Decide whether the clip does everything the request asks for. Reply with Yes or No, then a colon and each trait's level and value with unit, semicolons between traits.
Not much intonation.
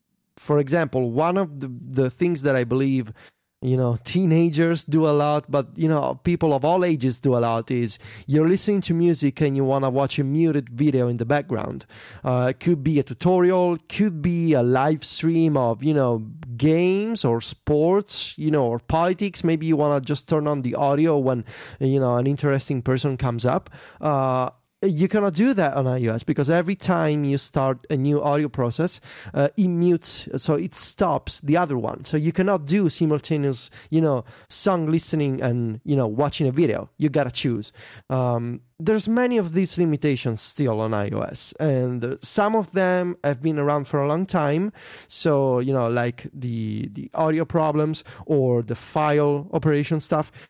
No: average, 4.3 semitones